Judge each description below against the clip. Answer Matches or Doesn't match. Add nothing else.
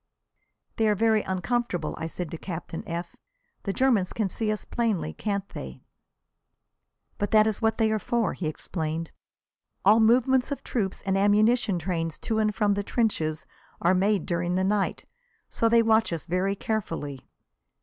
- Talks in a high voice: Matches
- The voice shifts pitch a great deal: Doesn't match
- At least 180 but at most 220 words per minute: Doesn't match